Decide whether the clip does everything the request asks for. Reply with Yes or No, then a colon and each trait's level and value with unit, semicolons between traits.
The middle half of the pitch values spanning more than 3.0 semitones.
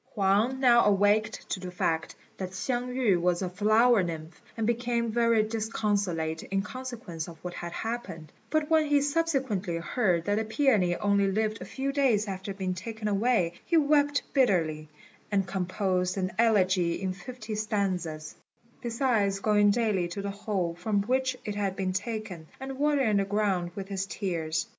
Yes: average, 4.4 semitones